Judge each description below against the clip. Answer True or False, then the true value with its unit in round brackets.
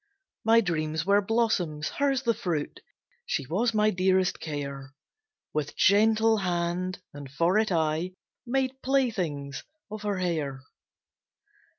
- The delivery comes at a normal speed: False (120 wpm)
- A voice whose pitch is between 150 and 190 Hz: True (185 Hz)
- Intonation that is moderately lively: False (6.1 semitones)